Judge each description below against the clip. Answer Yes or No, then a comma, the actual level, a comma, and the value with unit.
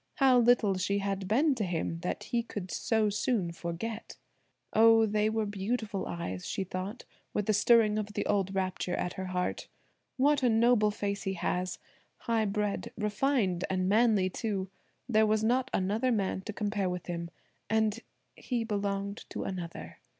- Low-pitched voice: No, high, 210 Hz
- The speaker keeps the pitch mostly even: No, average, 3.1 semitones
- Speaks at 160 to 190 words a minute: Yes, average, 165 wpm